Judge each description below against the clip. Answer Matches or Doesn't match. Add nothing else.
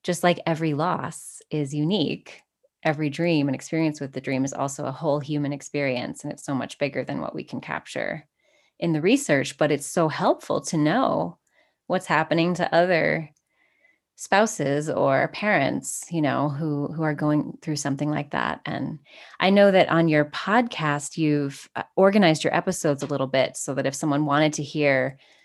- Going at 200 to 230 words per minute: Doesn't match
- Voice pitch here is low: Doesn't match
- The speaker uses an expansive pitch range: Doesn't match